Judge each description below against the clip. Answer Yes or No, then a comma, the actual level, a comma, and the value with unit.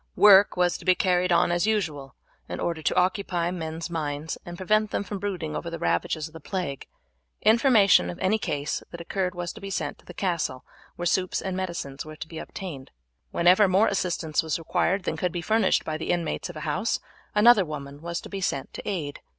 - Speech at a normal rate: No, fast, 215 wpm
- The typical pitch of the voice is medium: Yes, medium, 175 Hz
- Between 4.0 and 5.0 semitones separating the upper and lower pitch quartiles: No, average, 3.4 semitones